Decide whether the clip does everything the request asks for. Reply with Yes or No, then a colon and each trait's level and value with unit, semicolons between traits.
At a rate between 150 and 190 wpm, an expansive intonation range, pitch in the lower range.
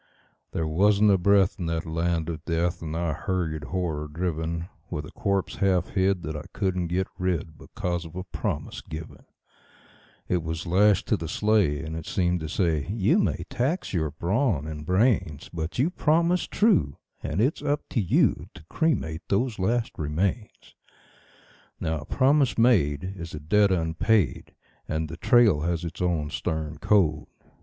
No: average, 165 wpm; average, 4.3 semitones; very low, 85 Hz